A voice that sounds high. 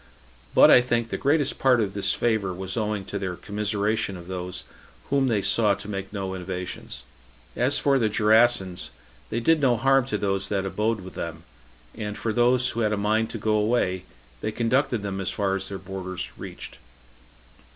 No: low, 105 Hz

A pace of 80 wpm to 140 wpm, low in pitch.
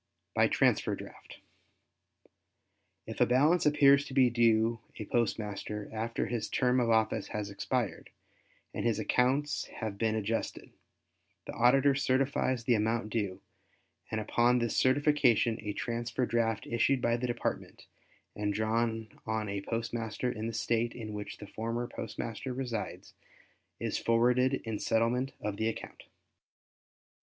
Yes: slow, 135 wpm; low, 115 Hz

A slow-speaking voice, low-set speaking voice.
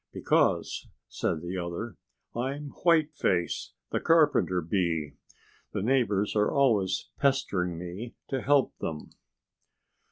Yes: slow, 105 wpm; low, 105 Hz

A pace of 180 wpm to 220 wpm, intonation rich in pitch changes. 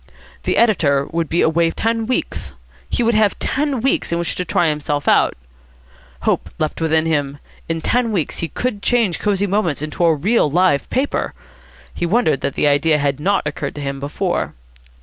Yes: average, 185 wpm; wide, 6.1 semitones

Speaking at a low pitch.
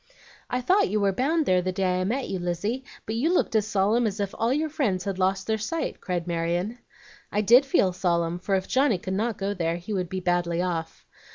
No: high, 195 Hz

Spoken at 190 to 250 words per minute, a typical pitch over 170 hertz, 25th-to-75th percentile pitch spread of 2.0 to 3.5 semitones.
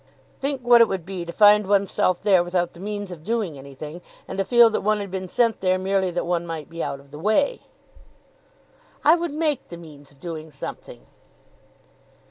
No: fast, 205 wpm; medium, 185 Hz; average, 4.2 semitones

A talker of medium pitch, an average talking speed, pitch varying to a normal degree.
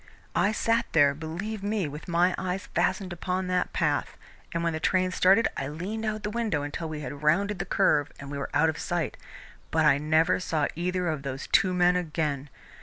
No: medium, 175 Hz; fast, 210 wpm; average, 3.8 semitones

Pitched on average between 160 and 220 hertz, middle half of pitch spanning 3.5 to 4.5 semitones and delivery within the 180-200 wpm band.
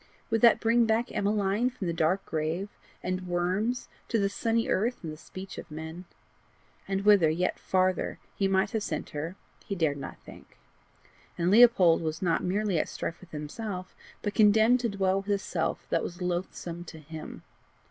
Yes: high, 190 Hz; average, 3.8 semitones; average, 185 wpm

